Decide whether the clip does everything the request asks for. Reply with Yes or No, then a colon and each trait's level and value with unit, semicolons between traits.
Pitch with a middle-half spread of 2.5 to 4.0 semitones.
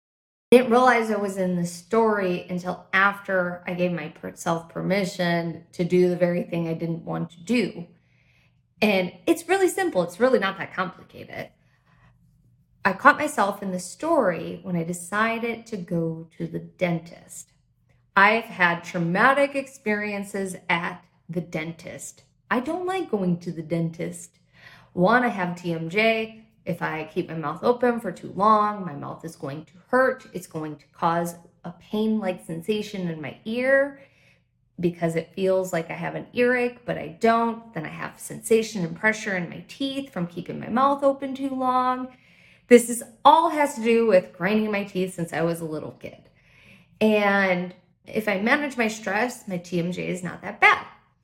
No: average, 4.9 semitones